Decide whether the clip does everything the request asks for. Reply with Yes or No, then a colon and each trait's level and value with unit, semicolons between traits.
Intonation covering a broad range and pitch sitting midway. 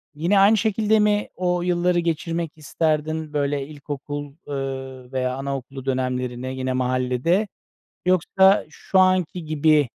No: average, 5.0 semitones; medium, 150 Hz